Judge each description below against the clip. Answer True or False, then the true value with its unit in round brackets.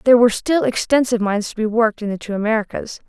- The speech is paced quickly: True (235 wpm)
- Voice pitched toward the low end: False (215 Hz)